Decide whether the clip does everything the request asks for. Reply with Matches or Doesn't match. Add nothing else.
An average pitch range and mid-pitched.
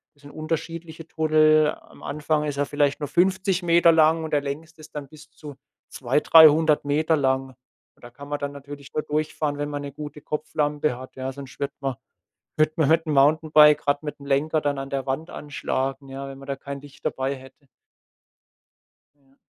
Doesn't match